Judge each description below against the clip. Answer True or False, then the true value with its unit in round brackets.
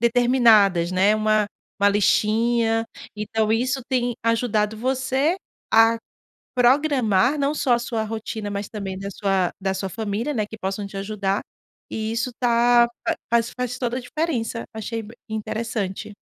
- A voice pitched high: True (225 Hz)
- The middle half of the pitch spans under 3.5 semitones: True (2.8 semitones)